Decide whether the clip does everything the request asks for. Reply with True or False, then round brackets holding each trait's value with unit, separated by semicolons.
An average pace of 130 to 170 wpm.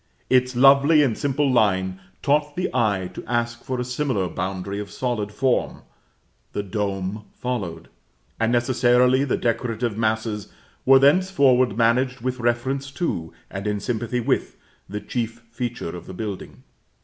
True (145 wpm)